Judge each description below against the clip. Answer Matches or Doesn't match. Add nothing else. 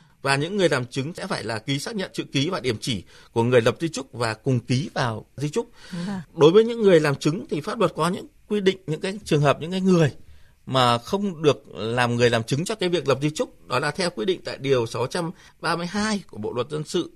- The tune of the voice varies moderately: Doesn't match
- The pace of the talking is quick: Matches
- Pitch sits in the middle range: Matches